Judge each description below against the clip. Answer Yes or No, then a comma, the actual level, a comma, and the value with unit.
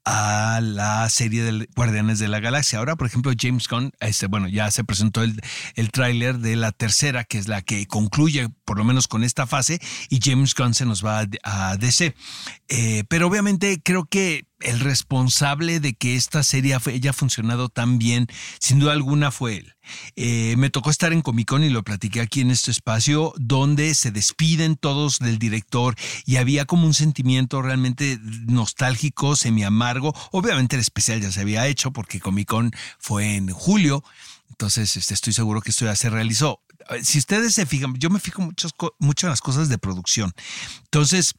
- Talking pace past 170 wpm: Yes, average, 185 wpm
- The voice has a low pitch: Yes, low, 125 Hz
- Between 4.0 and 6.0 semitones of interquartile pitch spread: Yes, average, 4.4 semitones